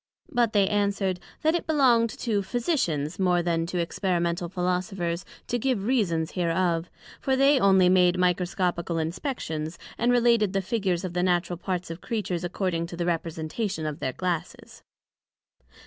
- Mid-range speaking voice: Yes, medium, 180 Hz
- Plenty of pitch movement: No, average, 3.6 semitones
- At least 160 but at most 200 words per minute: No, average, 150 wpm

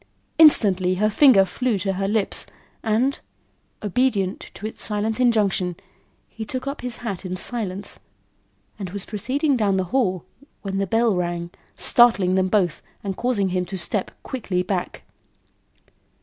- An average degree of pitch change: Yes, average, 4.1 semitones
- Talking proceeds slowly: No, average, 150 wpm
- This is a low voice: No, high, 200 Hz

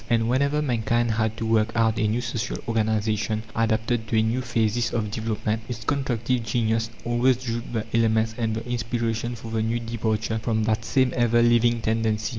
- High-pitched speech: No, low, 115 Hz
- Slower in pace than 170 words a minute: No, average, 185 wpm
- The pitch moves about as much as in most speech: No, narrow, 1.2 semitones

